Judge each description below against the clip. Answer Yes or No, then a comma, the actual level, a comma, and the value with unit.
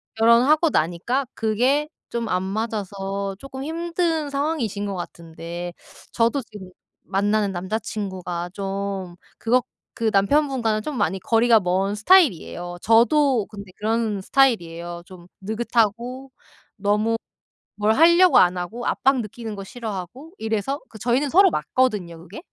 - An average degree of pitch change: Yes, average, 5.0 semitones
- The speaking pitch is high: Yes, high, 220 Hz